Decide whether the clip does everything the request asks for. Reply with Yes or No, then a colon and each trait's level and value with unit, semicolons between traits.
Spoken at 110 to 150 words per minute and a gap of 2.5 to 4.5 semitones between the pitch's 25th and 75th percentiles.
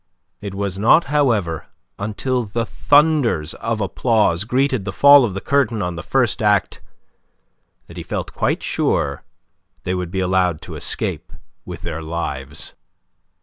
No: average, 145 wpm; wide, 5.6 semitones